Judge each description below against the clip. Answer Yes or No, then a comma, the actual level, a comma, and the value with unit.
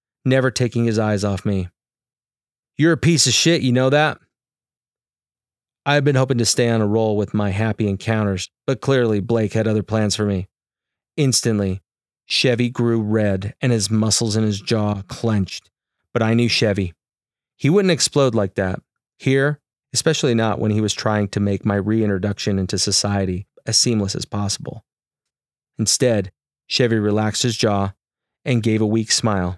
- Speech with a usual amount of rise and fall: Yes, average, 3.4 semitones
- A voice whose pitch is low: Yes, low, 110 Hz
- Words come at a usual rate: Yes, average, 165 wpm